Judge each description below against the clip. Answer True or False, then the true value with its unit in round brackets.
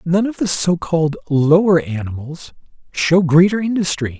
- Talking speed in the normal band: False (130 wpm)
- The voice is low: False (165 Hz)